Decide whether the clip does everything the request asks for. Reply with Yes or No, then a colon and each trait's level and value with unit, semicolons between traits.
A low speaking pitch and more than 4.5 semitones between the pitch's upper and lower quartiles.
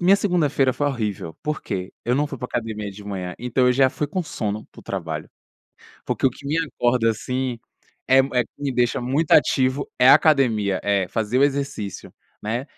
Yes: low, 125 Hz; average, 4.9 semitones